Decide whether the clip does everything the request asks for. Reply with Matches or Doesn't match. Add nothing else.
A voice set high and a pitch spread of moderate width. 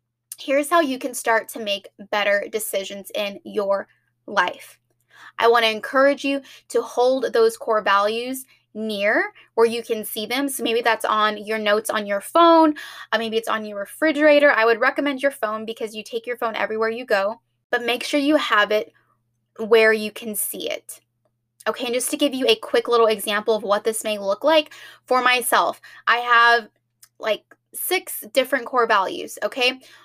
Matches